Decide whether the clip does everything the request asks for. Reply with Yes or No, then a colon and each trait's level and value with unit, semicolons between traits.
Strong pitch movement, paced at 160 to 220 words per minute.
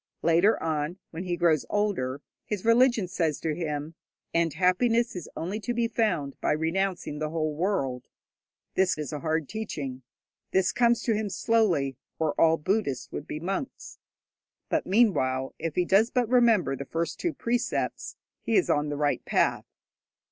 Yes: wide, 6.1 semitones; average, 165 wpm